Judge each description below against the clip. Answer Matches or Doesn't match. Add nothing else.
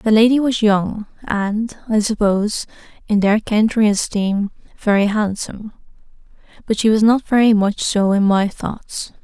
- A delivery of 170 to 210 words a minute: Doesn't match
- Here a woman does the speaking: Matches